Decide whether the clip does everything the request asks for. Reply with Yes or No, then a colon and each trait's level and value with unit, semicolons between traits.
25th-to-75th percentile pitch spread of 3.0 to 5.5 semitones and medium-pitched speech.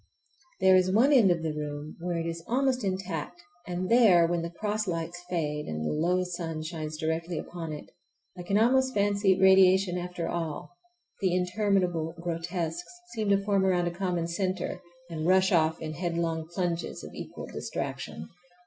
No: narrow, 2.6 semitones; medium, 175 Hz